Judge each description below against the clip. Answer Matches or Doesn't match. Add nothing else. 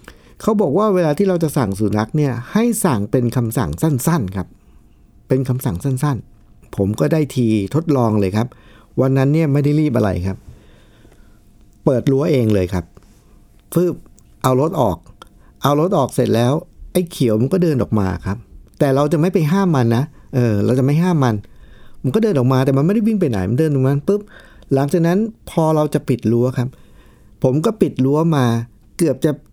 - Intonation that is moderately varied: Doesn't match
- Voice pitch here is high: Doesn't match